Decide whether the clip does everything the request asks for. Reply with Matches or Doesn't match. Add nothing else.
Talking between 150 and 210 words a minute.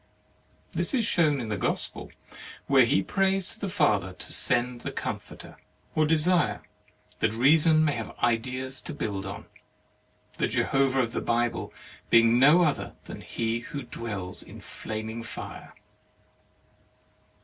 Doesn't match